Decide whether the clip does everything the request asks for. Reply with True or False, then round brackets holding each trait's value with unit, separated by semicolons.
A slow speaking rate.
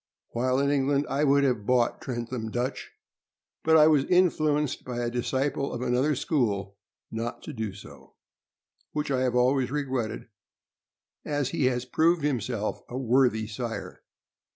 False (150 wpm)